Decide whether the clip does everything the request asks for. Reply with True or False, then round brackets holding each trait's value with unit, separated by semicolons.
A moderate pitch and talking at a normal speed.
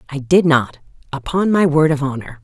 True (150 Hz; 195 wpm)